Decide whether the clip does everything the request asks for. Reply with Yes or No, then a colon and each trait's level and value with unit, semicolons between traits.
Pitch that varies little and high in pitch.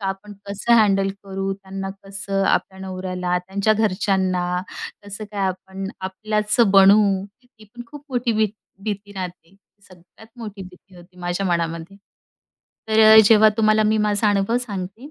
Yes: narrow, 2.3 semitones; high, 195 Hz